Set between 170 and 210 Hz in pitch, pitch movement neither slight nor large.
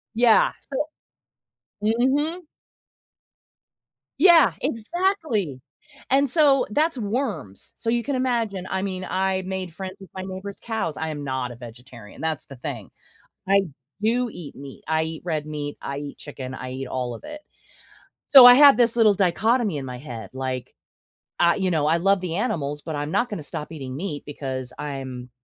No: medium, 185 Hz; wide, 8.7 semitones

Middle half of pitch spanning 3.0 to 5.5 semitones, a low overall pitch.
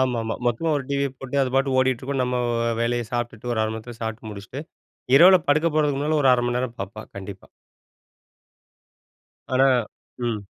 Yes: average, 3.4 semitones; low, 125 Hz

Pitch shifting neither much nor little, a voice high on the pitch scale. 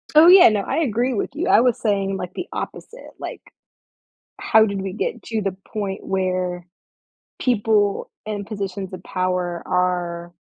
Yes: average, 3.4 semitones; high, 200 Hz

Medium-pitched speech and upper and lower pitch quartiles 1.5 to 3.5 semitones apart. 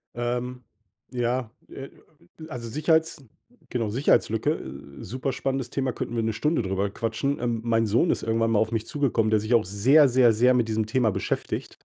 No: low, 120 Hz; average, 2.8 semitones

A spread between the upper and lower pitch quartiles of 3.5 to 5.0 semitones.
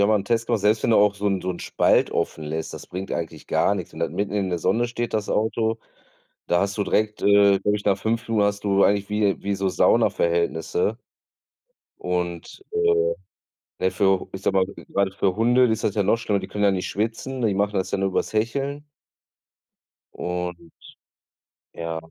No: average, 2.7 semitones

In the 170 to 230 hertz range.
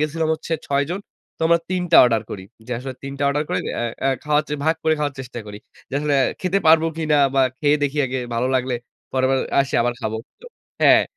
No: medium, 140 Hz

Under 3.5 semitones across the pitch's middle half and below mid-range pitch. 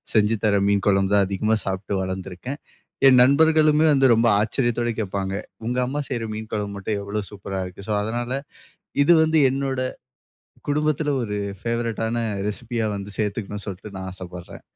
No: average, 4.1 semitones; low, 110 Hz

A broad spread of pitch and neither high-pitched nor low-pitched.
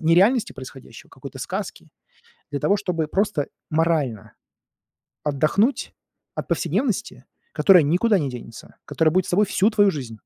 Yes: wide, 5.8 semitones; medium, 165 Hz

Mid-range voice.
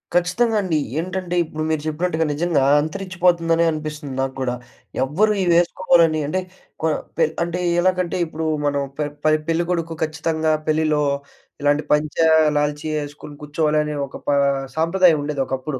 Yes: medium, 160 Hz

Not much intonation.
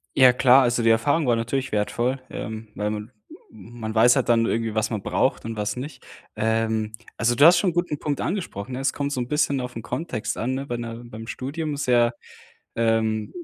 No: average, 3.3 semitones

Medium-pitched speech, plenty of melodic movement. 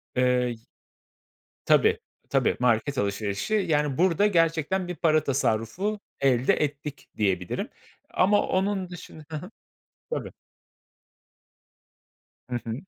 Yes: medium, 150 Hz; wide, 6.6 semitones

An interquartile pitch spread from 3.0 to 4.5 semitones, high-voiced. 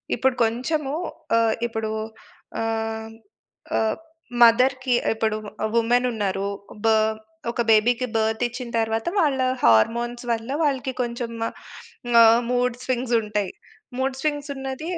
No: narrow, 2.4 semitones; high, 235 Hz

